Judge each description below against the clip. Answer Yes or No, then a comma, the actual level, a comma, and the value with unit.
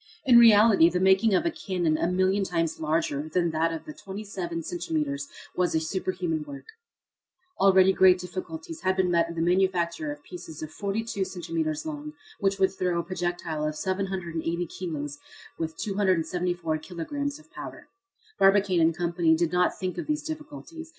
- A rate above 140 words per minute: Yes, average, 165 wpm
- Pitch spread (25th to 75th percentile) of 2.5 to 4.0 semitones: Yes, average, 3.1 semitones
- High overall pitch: No, medium, 180 Hz